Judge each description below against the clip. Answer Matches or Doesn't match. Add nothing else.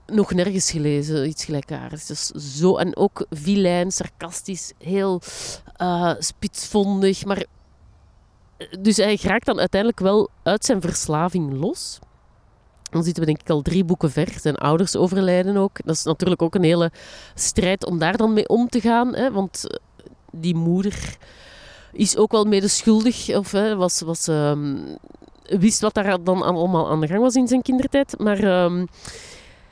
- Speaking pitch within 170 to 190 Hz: Matches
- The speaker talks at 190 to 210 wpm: Doesn't match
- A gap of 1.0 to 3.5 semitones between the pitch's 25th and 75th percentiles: Doesn't match